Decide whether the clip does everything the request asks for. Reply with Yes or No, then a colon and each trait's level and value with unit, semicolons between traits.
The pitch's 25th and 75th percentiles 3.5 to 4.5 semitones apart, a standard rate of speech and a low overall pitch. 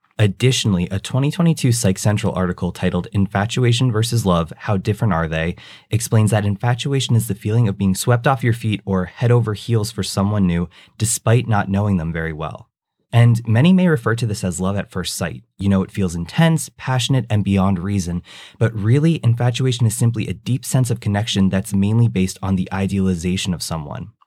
Yes: average, 3.8 semitones; average, 190 wpm; low, 105 Hz